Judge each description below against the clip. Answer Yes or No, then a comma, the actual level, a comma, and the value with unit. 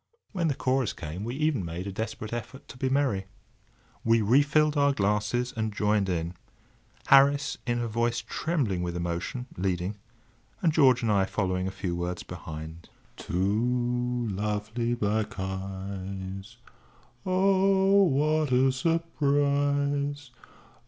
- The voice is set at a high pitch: No, low, 120 Hz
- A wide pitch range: Yes, wide, 6.7 semitones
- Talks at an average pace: No, slow, 130 wpm